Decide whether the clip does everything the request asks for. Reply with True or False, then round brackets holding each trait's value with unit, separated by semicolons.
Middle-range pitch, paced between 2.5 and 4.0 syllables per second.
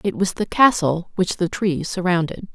False (180 Hz; 4.7 syllables/s)